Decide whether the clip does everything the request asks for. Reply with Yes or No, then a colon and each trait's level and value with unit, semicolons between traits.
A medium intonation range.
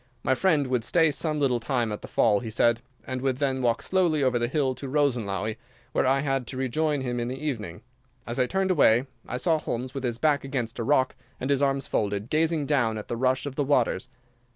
Yes: average, 3.4 semitones